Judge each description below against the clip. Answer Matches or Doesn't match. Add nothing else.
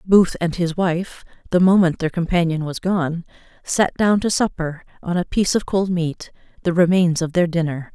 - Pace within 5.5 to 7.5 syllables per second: Doesn't match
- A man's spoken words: Doesn't match